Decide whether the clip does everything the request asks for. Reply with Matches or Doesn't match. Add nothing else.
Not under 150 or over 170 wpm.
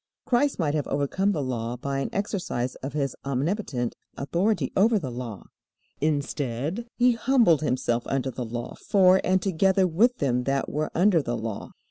Matches